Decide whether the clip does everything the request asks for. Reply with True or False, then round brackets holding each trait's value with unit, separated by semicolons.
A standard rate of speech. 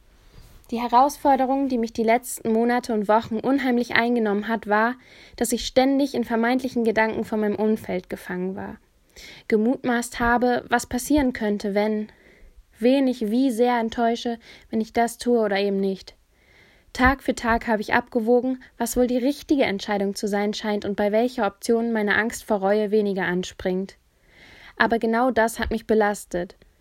True (160 wpm)